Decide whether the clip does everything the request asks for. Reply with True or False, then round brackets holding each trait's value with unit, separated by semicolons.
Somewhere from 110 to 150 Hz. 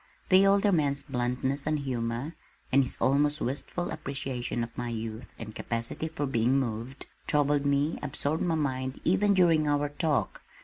True (140 Hz)